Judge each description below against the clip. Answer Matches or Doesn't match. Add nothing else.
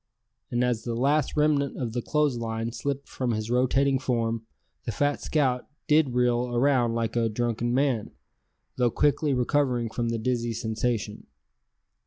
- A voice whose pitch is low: Matches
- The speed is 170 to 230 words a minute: Doesn't match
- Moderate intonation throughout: Matches